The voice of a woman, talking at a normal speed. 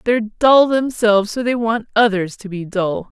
Yes: female; average, 190 wpm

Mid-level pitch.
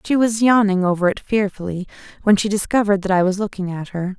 No: high, 200 Hz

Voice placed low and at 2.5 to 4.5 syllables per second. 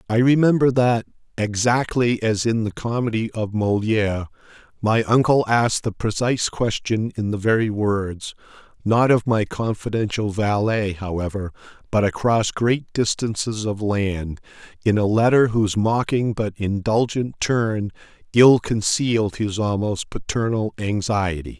Yes: low, 110 Hz; 4.4 syllables/s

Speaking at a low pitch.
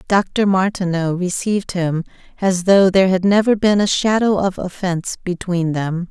No: medium, 185 Hz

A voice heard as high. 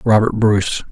No: low, 105 Hz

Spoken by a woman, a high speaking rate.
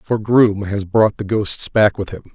No: male; fast, 230 wpm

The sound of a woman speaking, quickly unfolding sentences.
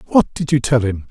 No: male; fast, 270 wpm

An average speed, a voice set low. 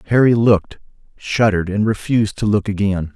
Yes: average, 150 wpm; low, 105 Hz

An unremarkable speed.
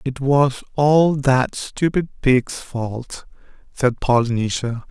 No: slow, 110 wpm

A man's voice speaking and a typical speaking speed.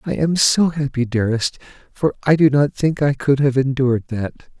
Yes: male; average, 195 wpm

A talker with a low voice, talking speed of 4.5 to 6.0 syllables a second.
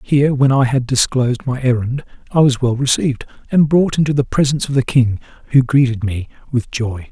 Yes: low, 130 Hz; 5.7 syllables/s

